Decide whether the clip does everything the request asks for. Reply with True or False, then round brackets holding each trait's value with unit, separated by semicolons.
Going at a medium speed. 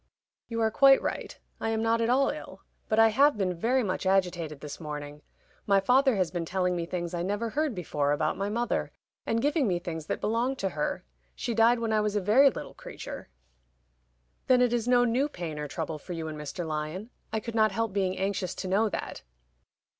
False (215 wpm)